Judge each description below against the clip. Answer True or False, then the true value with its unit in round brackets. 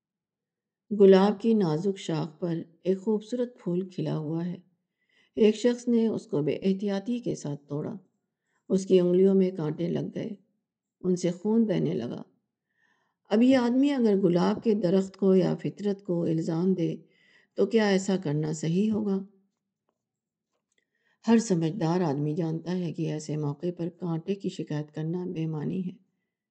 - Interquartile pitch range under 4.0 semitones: True (3.5 semitones)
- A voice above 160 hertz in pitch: True (190 Hz)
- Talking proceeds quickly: False (155 wpm)